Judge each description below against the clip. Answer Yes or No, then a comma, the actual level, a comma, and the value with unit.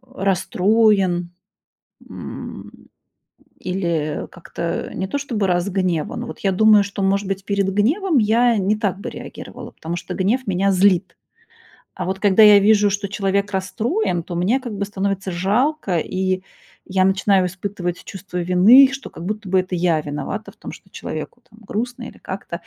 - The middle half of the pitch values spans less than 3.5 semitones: Yes, narrow, 2.4 semitones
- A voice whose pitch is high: Yes, high, 195 Hz